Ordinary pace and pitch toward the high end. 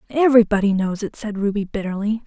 Yes: average, 160 wpm; high, 210 Hz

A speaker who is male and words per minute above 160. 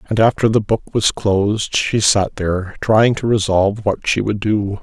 Yes: male; average, 200 wpm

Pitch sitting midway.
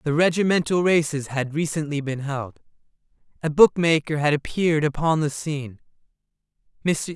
Yes: medium, 150 Hz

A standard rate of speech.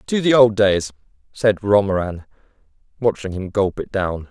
Yes: average, 155 wpm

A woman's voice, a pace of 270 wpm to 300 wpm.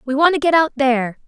Yes: female; fast, 285 wpm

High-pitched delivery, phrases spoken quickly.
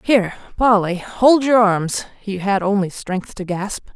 No: high, 200 Hz; average, 165 wpm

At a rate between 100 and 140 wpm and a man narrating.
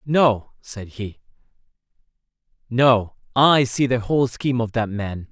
Yes: slow, 135 wpm; male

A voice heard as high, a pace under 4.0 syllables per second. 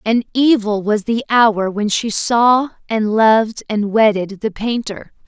Yes: high, 220 Hz; 3.8 syllables/s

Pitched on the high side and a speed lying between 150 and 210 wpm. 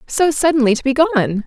Yes: very high, 270 Hz; fast, 205 wpm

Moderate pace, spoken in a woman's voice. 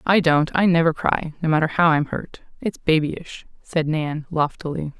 Yes: average, 180 wpm; female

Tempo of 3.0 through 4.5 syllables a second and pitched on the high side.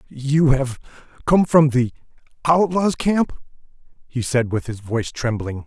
No: 4.1 syllables/s; low, 135 Hz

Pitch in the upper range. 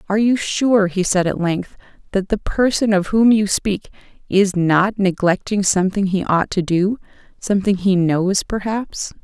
Yes: high, 195 Hz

